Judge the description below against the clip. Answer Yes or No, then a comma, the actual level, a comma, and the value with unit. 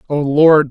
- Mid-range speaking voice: Yes, medium, 145 Hz